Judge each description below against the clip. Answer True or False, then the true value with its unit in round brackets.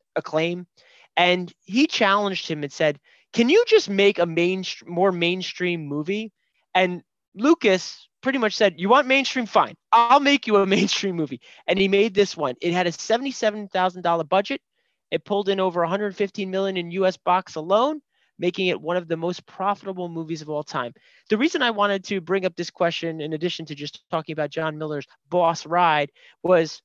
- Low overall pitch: False (185 Hz)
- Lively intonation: False (3.4 semitones)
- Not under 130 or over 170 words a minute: False (190 wpm)